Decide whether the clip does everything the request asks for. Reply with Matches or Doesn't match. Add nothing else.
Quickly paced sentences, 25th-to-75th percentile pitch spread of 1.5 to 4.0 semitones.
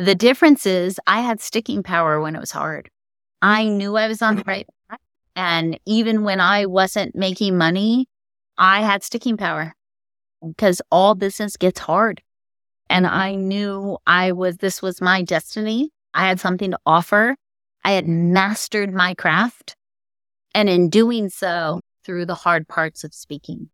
Doesn't match